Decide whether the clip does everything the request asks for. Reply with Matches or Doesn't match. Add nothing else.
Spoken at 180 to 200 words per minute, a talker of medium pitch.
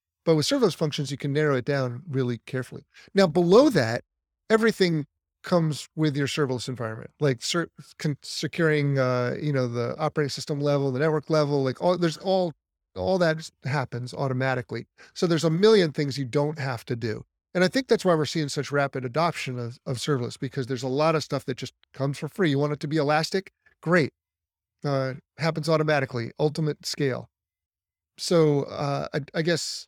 Matches